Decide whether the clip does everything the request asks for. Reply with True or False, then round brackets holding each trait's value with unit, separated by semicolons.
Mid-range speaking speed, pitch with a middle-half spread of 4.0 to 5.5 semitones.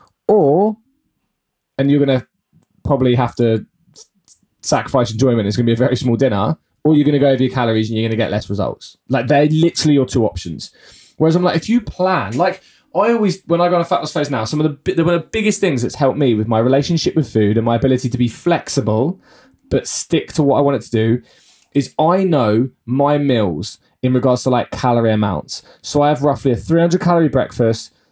False (225 wpm; 5.1 semitones)